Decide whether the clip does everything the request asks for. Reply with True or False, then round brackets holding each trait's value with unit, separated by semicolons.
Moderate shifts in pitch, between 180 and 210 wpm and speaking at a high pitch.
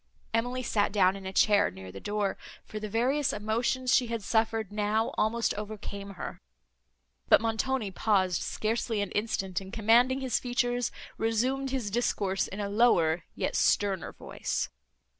False (3.2 semitones; 155 wpm; 215 Hz)